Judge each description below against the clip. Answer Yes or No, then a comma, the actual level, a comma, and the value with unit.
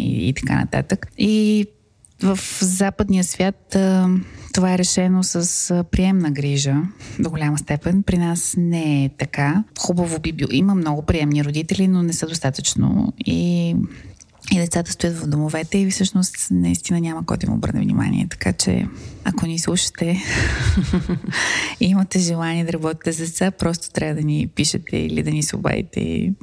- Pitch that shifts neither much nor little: Yes, average, 4.1 semitones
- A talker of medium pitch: Yes, medium, 170 Hz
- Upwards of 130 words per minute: Yes, average, 155 wpm